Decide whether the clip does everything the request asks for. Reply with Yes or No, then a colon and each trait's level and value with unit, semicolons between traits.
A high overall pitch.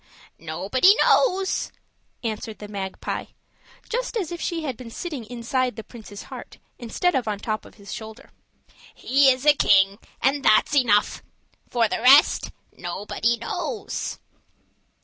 Yes: high, 240 Hz